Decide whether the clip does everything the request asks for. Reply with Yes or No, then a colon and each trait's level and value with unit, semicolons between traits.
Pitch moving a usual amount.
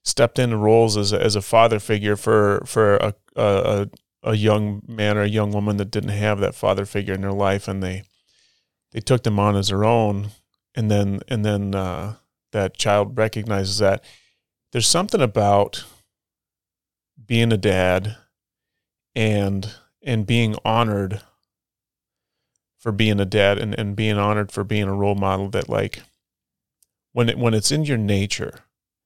No: narrow, 1.7 semitones